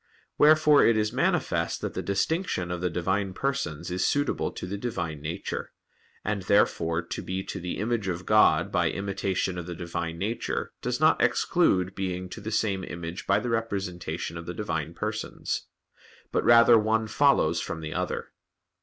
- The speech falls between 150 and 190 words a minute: Yes, average, 170 wpm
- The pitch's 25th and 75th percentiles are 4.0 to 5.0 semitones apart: Yes, average, 4.3 semitones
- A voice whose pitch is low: Yes, very low, 95 Hz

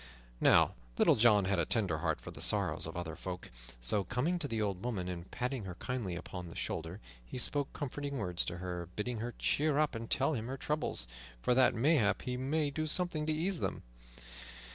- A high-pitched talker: No, low, 115 Hz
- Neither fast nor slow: No, fast, 210 wpm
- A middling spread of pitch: No, wide, 7.8 semitones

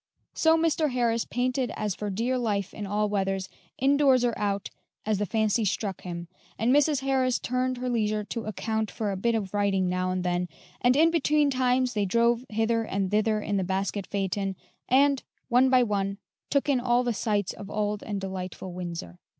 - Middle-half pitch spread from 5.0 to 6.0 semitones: No, average, 4.2 semitones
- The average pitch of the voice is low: No, high, 215 Hz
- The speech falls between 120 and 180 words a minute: No, average, 190 wpm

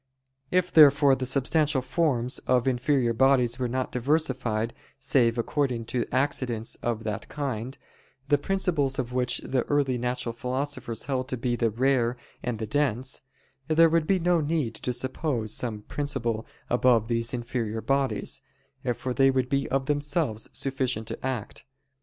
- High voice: No, low, 130 Hz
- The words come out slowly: No, average, 155 wpm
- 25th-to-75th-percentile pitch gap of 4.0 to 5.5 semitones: No, average, 3.1 semitones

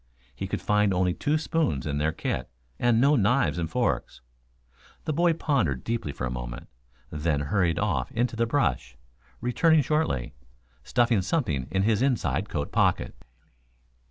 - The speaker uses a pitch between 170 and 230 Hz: No, low, 105 Hz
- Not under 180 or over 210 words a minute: No, average, 155 wpm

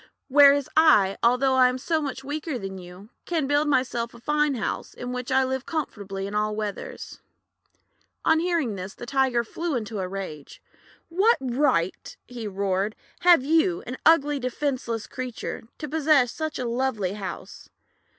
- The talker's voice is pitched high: Yes, very high, 255 Hz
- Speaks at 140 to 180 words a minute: Yes, average, 170 wpm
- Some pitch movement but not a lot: No, wide, 5.7 semitones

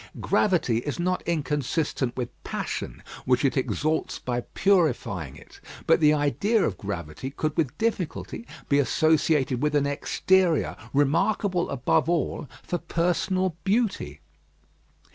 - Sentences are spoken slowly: Yes, slow, 125 wpm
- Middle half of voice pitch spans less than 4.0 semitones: No, average, 5.3 semitones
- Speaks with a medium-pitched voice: Yes, medium, 150 Hz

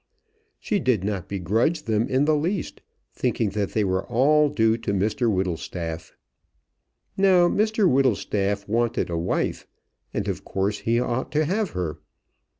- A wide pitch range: Yes, wide, 7.4 semitones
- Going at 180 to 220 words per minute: No, average, 150 wpm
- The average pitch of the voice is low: Yes, low, 115 Hz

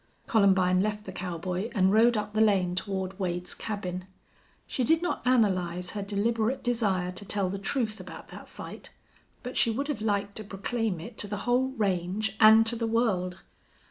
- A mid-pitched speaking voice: No, high, 205 Hz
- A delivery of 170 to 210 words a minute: Yes, average, 180 wpm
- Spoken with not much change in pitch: No, average, 3.4 semitones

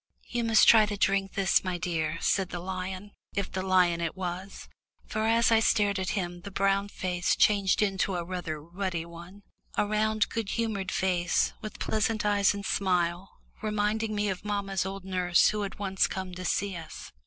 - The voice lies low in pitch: No, high, 195 Hz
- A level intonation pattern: Yes, narrow, 2.3 semitones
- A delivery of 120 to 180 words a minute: No, average, 190 wpm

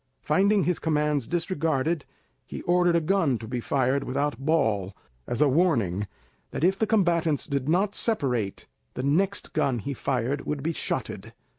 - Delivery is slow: No, average, 160 wpm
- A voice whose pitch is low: No, medium, 150 Hz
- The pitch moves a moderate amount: Yes, average, 4.9 semitones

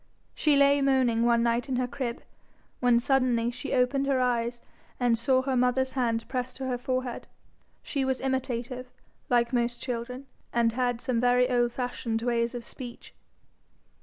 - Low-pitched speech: No, very high, 250 Hz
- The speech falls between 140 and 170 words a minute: Yes, average, 165 wpm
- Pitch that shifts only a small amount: Yes, narrow, 1.6 semitones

